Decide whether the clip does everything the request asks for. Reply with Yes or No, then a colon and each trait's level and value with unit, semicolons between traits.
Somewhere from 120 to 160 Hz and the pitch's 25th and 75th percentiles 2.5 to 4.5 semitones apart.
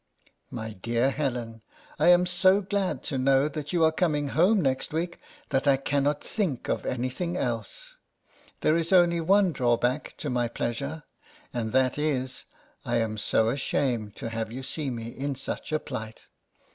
No: medium, 140 Hz; average, 5.3 semitones